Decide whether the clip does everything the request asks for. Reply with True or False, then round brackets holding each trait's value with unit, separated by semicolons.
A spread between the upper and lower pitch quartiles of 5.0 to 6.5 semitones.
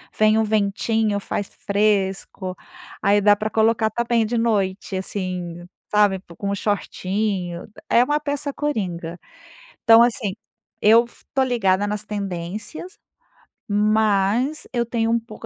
False (2.8 semitones)